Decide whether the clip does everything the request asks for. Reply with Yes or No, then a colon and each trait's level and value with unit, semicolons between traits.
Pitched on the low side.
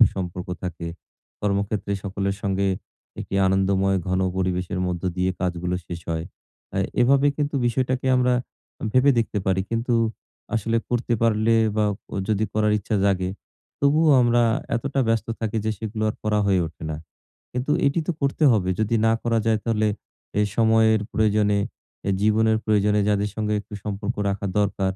Yes: low, 105 Hz